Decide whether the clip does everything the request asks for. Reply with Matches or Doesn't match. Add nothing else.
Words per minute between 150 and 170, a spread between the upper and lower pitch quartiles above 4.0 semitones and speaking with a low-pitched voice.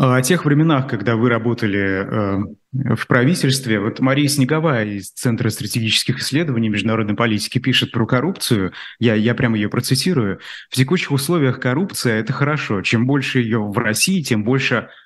Doesn't match